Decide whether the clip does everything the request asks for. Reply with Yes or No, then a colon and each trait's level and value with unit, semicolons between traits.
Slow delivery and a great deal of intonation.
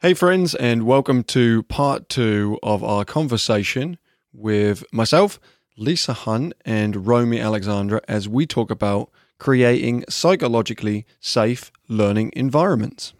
No: slow, 120 wpm; average, 4.4 semitones